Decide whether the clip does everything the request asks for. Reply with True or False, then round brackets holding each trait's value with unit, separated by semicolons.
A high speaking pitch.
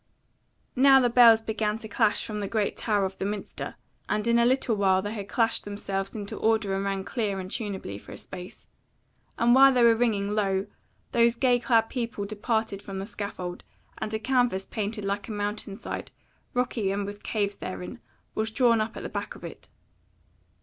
True (210 Hz)